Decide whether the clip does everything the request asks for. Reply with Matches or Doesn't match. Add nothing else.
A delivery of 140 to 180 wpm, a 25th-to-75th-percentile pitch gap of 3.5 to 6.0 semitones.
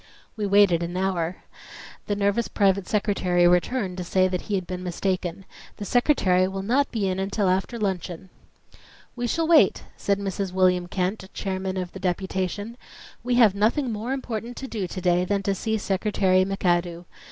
Doesn't match